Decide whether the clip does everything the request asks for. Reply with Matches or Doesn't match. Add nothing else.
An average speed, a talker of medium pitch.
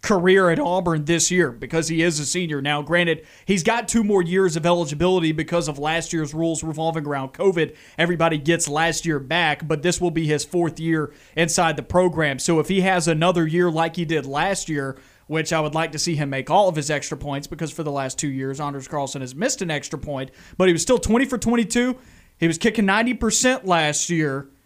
Doesn't match